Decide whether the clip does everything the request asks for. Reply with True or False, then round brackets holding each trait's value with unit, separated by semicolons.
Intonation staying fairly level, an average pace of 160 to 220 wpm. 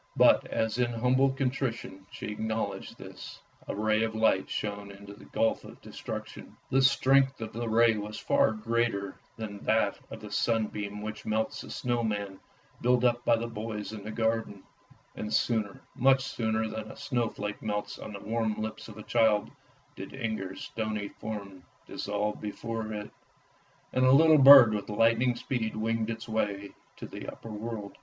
True (1.9 semitones; 170 wpm)